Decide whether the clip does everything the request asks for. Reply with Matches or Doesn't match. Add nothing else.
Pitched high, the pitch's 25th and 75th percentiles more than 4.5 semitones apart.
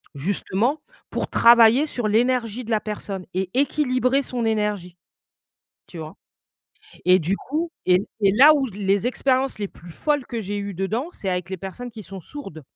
Matches